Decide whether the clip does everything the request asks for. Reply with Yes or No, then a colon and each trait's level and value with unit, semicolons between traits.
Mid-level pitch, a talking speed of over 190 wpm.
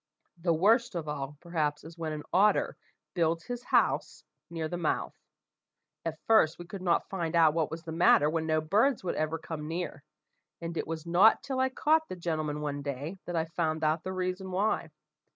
Yes: medium, 165 Hz; average, 200 wpm